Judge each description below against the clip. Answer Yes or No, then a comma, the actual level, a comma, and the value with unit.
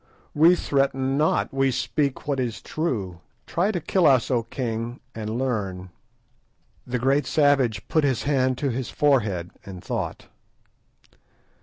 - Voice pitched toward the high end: No, low, 130 Hz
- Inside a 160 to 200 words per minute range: No, average, 140 wpm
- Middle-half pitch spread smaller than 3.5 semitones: No, average, 4.0 semitones